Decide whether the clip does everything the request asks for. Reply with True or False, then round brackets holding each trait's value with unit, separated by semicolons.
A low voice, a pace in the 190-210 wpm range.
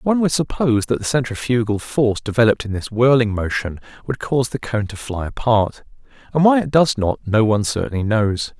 True (120 Hz; 195 wpm)